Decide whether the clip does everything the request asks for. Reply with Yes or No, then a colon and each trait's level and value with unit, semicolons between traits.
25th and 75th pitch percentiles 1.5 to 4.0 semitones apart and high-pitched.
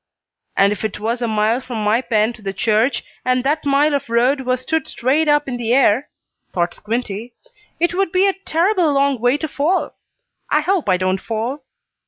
No: average, 5.0 semitones; very high, 255 Hz